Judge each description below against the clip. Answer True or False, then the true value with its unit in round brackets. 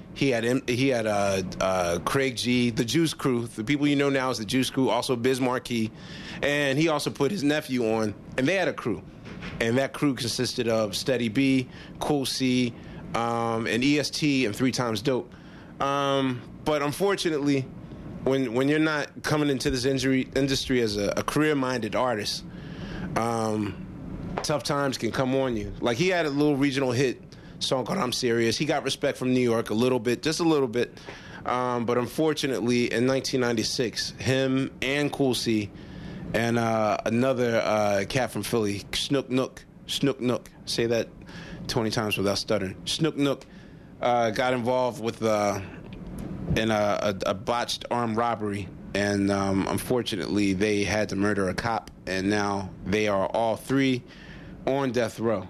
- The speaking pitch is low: True (125 Hz)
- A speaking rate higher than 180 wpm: False (170 wpm)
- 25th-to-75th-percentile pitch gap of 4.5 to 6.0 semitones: False (3.8 semitones)